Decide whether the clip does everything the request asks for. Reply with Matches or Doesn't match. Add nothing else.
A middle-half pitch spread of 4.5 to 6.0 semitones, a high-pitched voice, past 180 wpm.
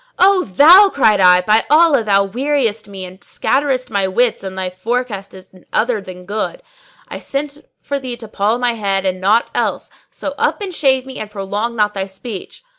Matches